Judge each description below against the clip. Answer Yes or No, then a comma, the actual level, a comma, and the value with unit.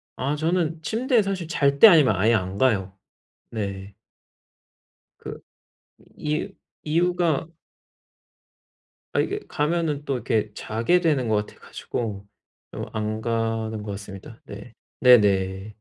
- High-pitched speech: No, low, 120 Hz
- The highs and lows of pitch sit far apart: Yes, wide, 7.4 semitones